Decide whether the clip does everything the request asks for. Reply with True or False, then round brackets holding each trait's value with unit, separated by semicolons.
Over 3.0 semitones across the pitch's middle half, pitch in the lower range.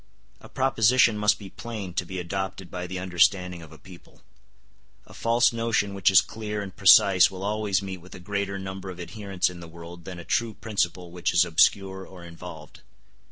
False (2.6 semitones; 95 Hz)